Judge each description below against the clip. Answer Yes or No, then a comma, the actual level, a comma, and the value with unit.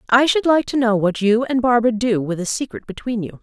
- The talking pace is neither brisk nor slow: No, fast, 265 wpm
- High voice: Yes, high, 230 Hz